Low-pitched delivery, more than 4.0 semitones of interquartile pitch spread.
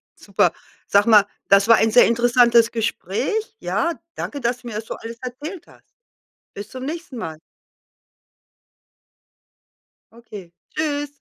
No: high, 235 Hz; average, 4.7 semitones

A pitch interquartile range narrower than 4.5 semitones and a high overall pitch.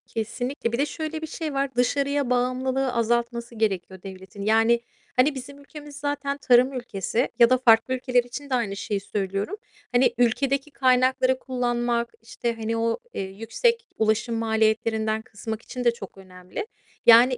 Yes: average, 3.0 semitones; high, 240 Hz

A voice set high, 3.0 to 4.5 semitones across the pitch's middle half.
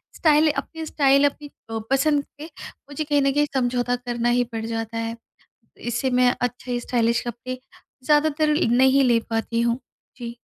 Yes: very high, 250 Hz; average, 3.4 semitones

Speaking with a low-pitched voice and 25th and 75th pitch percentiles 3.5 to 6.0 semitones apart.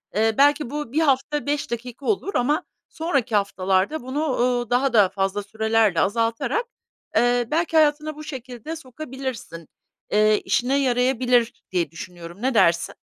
No: high, 245 Hz; average, 5.2 semitones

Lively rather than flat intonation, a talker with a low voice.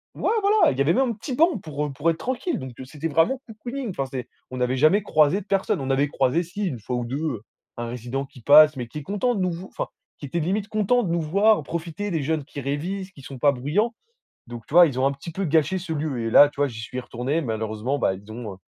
No: wide, 6.4 semitones; medium, 150 Hz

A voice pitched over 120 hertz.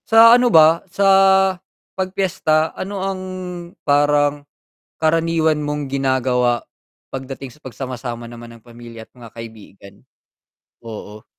Yes: medium, 140 Hz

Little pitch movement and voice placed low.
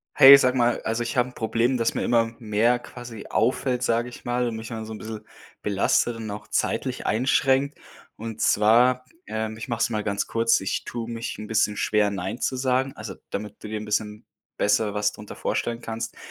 Yes: narrow, 2.3 semitones; low, 115 Hz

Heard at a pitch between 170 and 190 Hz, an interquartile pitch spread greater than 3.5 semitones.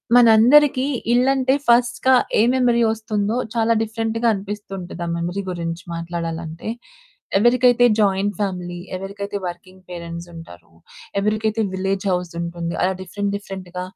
No: high, 200 Hz; average, 4.2 semitones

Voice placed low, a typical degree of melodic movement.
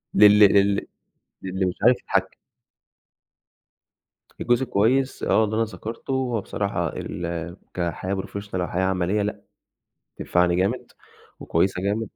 Yes: low, 100 Hz; average, 3.2 semitones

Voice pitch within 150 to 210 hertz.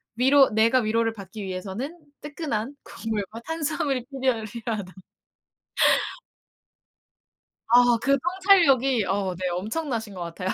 No: high, 230 Hz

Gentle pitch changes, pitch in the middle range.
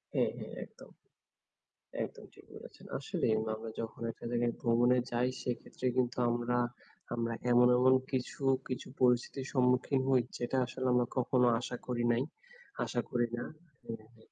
No: narrow, 1.1 semitones; low, 125 Hz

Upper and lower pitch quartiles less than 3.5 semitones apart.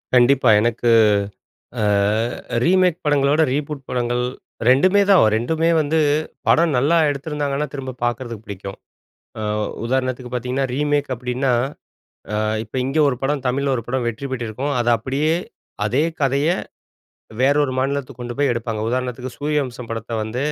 Yes: average, 3.1 semitones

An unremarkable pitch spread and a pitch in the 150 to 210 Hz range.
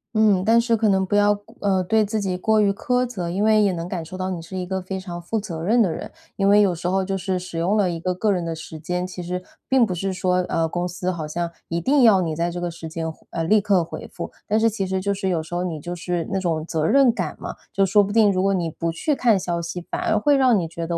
Yes: average, 3.2 semitones; medium, 185 Hz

